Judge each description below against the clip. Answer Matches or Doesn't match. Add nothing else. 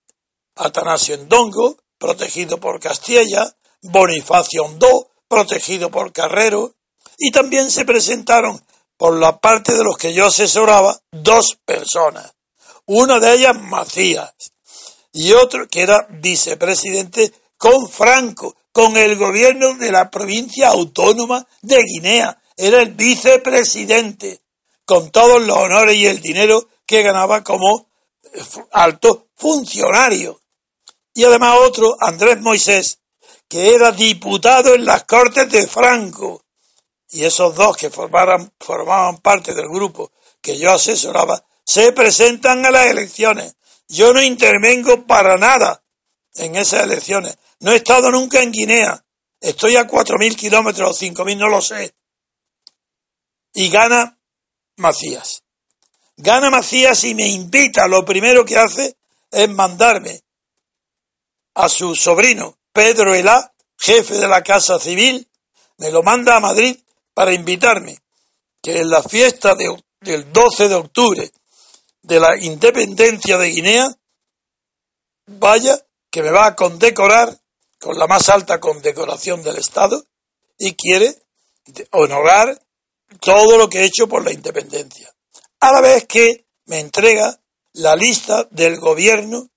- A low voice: Doesn't match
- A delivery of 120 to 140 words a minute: Matches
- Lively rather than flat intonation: Doesn't match